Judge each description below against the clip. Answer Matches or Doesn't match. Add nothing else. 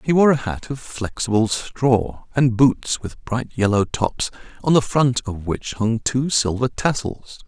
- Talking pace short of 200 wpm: Matches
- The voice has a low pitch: Matches